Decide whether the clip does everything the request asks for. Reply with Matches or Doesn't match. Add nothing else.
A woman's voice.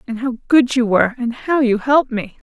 Matches